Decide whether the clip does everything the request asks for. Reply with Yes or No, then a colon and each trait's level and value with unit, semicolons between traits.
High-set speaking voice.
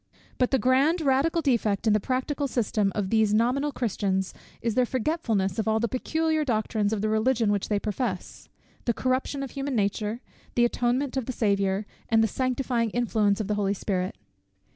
Yes: high, 230 Hz